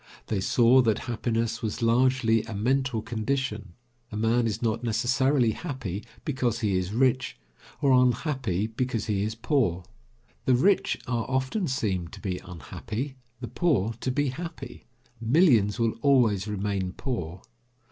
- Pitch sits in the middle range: No, low, 115 Hz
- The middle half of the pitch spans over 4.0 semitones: No, average, 3.6 semitones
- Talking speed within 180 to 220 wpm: No, average, 145 wpm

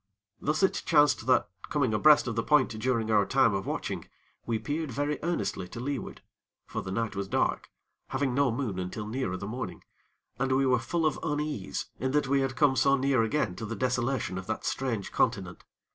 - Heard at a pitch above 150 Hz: No, low, 130 Hz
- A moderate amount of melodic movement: Yes, average, 4.5 semitones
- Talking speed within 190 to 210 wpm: Yes, average, 200 wpm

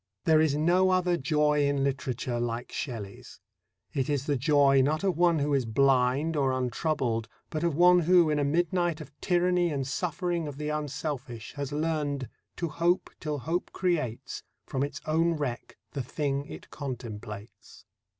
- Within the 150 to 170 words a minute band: Yes, average, 165 wpm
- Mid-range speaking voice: Yes, medium, 145 Hz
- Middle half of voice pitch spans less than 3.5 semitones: No, average, 3.8 semitones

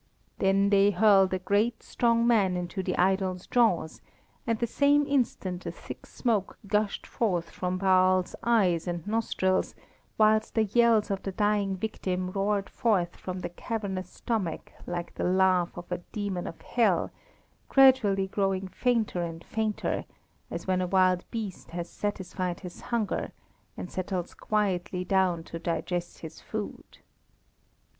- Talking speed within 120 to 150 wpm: Yes, average, 145 wpm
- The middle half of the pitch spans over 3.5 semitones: No, average, 3.0 semitones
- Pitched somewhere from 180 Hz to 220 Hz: Yes, high, 190 Hz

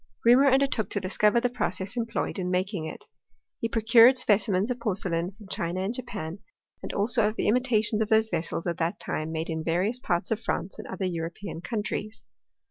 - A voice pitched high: Yes, high, 205 Hz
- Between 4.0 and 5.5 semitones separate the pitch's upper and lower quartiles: Yes, average, 4.4 semitones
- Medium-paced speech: Yes, average, 190 wpm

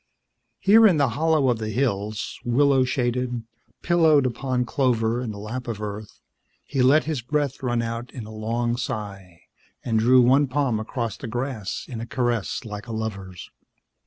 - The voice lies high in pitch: No, low, 120 Hz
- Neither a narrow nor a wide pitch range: Yes, average, 3.3 semitones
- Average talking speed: Yes, average, 170 wpm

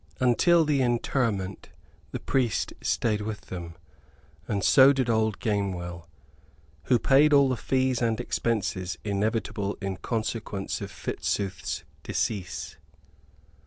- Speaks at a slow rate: Yes, slow, 115 wpm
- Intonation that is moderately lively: Yes, average, 4.5 semitones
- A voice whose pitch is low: Yes, low, 110 Hz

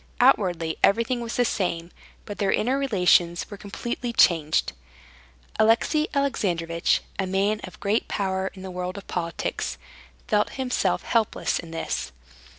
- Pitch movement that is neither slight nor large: Yes, average, 4.8 semitones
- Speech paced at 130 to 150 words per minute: Yes, average, 140 wpm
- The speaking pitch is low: No, high, 195 Hz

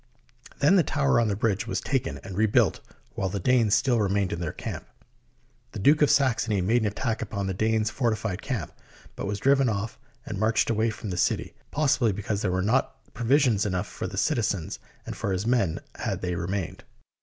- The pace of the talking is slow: No, average, 200 wpm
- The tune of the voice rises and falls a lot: No, average, 3.8 semitones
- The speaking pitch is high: No, low, 110 Hz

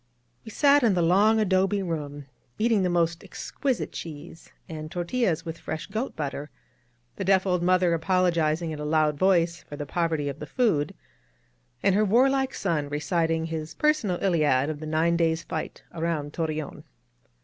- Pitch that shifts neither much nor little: Yes, average, 3.8 semitones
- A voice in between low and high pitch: Yes, medium, 170 Hz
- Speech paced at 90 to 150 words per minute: No, average, 170 wpm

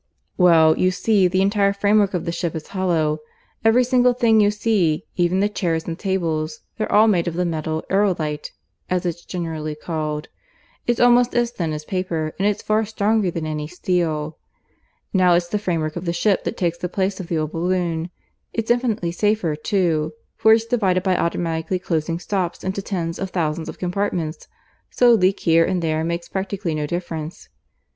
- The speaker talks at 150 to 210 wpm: Yes, average, 185 wpm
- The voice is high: No, medium, 180 Hz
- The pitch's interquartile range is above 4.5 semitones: No, average, 3.8 semitones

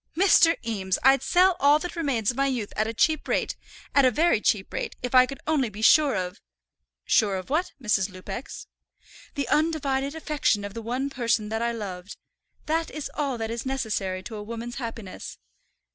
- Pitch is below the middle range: No, high, 240 Hz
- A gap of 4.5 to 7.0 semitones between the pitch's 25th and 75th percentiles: Yes, average, 5.2 semitones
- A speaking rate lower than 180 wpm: No, average, 195 wpm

